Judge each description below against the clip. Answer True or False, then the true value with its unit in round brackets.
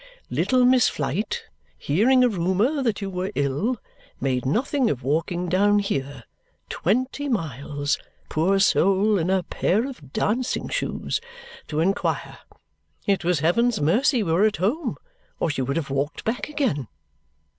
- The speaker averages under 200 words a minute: True (145 wpm)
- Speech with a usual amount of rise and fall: False (7.6 semitones)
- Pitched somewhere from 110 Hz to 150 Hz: False (190 Hz)